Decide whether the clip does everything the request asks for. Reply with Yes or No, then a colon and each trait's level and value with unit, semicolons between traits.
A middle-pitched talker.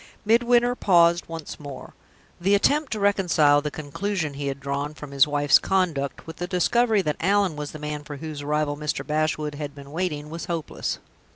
Yes: medium, 155 Hz